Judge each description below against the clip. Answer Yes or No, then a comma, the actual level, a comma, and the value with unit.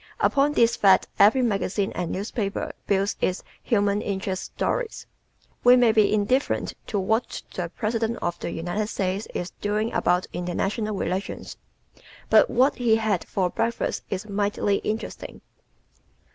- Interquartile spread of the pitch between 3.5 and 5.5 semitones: No, average, 2.9 semitones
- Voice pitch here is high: Yes, high, 205 Hz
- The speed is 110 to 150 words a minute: Yes, average, 140 wpm